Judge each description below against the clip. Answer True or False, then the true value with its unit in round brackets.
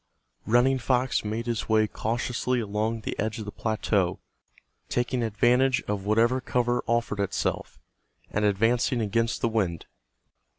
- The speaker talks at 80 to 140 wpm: True (135 wpm)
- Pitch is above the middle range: False (115 Hz)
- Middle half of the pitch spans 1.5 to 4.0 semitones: True (2.5 semitones)